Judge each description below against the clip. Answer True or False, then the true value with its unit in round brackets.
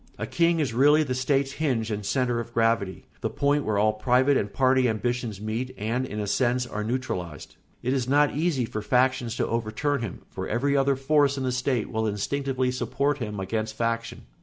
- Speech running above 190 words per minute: True (200 wpm)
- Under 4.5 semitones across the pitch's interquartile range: True (3.7 semitones)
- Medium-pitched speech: False (125 Hz)